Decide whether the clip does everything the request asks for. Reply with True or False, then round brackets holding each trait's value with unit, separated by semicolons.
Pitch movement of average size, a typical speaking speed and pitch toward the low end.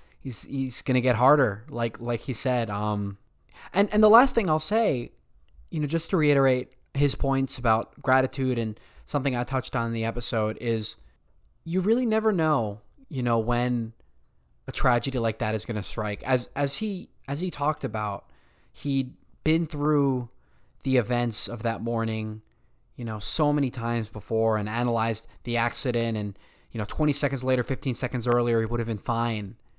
True (3.6 semitones; 175 wpm; 120 Hz)